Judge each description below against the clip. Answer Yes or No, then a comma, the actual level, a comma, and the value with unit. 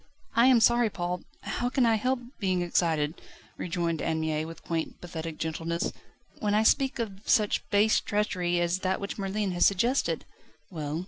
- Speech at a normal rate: Yes, average, 170 wpm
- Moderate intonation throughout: Yes, average, 4.5 semitones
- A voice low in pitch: No, medium, 185 Hz